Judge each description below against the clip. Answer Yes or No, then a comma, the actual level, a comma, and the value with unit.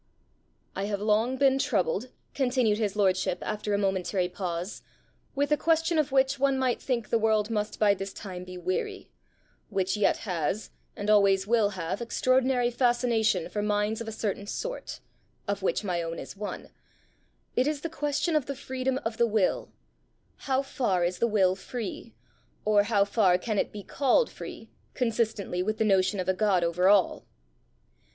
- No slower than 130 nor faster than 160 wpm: No, average, 175 wpm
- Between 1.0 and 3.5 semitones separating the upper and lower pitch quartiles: No, average, 4.6 semitones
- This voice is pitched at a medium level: No, high, 215 Hz